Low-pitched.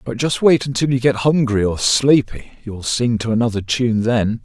Yes: low, 120 Hz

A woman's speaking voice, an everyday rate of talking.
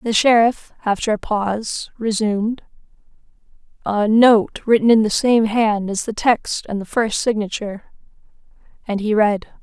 Yes: female; average, 145 wpm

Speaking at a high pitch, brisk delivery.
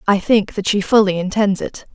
Yes: high, 200 Hz; fast, 215 wpm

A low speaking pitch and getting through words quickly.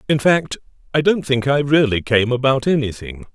No: low, 130 Hz; average, 180 wpm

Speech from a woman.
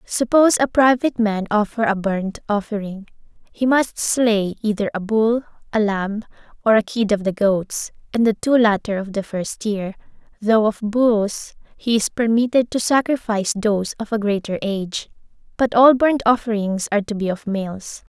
Yes: female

